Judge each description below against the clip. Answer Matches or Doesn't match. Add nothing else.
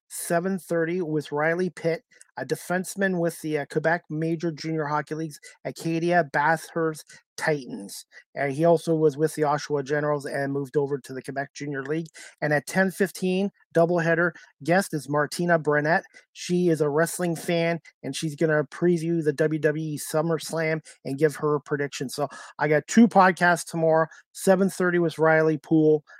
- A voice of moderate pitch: Matches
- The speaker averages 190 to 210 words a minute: Doesn't match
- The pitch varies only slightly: Matches